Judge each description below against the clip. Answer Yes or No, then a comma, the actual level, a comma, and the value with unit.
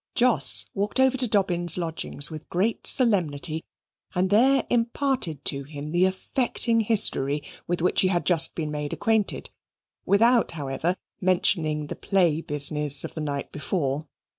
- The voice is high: No, medium, 175 Hz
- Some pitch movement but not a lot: No, wide, 6.0 semitones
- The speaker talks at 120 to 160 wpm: Yes, average, 145 wpm